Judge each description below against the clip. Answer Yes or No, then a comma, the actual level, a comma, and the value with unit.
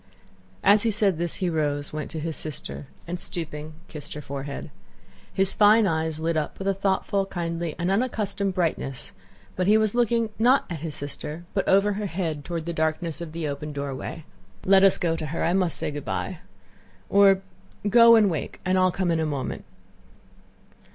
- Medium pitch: Yes, medium, 170 Hz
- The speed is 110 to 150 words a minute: No, average, 185 wpm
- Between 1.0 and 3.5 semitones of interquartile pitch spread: No, average, 4.0 semitones